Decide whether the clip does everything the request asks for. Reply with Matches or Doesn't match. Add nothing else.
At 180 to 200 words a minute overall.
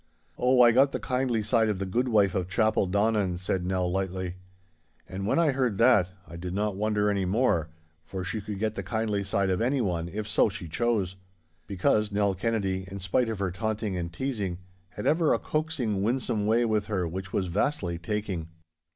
Matches